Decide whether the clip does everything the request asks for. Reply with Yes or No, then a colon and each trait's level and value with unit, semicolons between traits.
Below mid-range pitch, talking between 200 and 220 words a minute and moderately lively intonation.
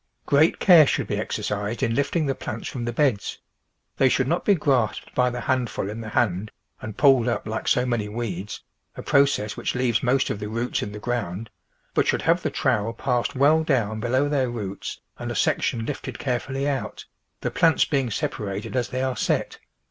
Yes: low, 120 Hz; fast, 205 wpm; average, 3.9 semitones